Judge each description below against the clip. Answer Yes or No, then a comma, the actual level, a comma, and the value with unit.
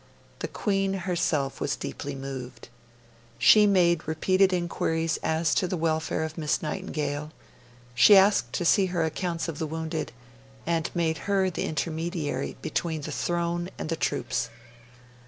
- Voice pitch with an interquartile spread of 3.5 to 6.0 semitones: No, narrow, 2.5 semitones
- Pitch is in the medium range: Yes, medium, 165 Hz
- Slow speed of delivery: No, average, 145 wpm